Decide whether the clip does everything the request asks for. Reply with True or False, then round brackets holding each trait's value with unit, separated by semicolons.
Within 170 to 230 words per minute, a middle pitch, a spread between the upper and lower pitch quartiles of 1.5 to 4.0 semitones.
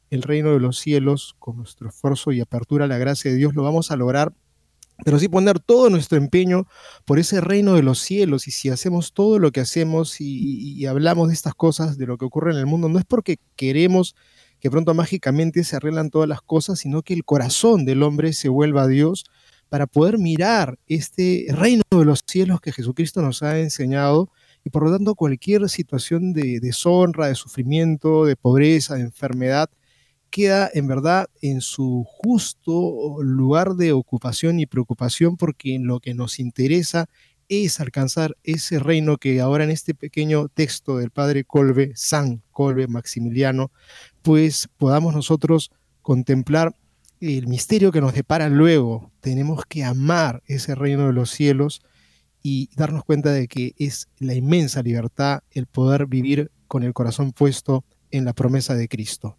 True (175 wpm; 145 Hz; 3.6 semitones)